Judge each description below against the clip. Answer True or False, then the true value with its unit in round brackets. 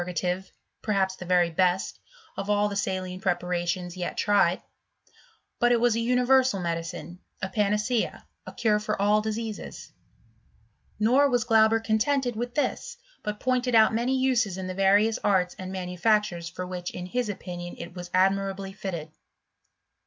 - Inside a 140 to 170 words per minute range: True (155 wpm)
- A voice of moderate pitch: False (200 Hz)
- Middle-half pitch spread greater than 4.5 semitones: False (3.8 semitones)